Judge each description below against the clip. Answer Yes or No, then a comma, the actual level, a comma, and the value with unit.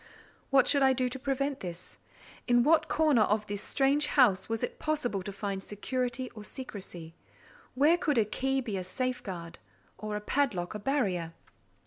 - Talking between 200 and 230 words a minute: No, average, 170 wpm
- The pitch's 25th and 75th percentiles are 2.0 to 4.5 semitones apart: No, average, 5.2 semitones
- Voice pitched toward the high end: Yes, high, 240 Hz